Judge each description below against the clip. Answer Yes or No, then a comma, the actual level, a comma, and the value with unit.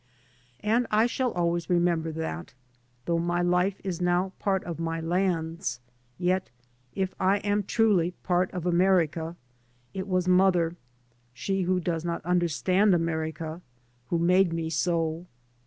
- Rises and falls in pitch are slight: Yes, narrow, 2.2 semitones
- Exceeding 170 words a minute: No, average, 140 wpm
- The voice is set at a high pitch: No, medium, 175 Hz